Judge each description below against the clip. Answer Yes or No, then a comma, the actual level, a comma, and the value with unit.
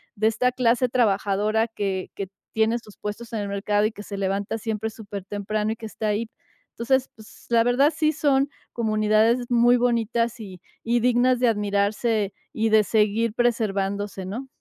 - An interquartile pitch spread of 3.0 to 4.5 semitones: No, narrow, 2.5 semitones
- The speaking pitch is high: Yes, high, 220 Hz